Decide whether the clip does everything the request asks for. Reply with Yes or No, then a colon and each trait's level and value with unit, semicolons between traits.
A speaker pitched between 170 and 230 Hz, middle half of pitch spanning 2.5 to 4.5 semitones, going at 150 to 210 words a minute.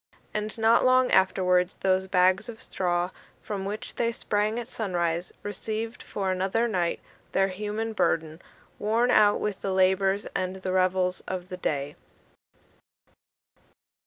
No: high, 190 Hz; average, 2.8 semitones; slow, 135 wpm